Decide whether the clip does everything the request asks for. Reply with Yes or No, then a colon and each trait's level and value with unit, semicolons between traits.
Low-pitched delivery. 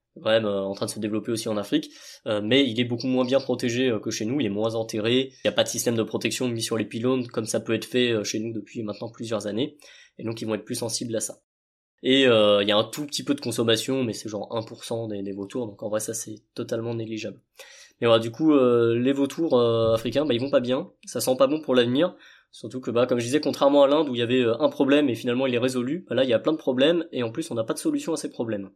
Yes: low, 120 Hz